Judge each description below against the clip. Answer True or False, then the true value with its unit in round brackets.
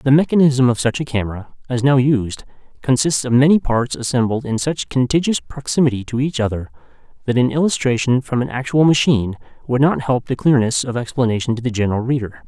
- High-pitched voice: False (125 Hz)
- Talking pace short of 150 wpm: False (190 wpm)